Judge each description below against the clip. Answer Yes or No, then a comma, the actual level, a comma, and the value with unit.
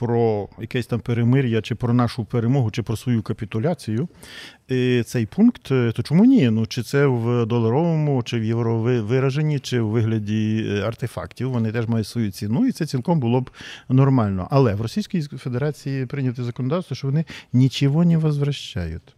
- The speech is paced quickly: Yes, fast, 160 wpm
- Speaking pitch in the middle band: No, low, 125 Hz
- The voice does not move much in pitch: No, average, 3.2 semitones